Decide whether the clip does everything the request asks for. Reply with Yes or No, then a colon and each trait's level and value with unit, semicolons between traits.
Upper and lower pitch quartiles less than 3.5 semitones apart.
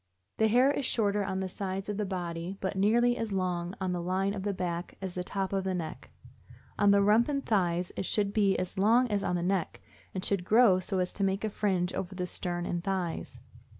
Yes: narrow, 2.4 semitones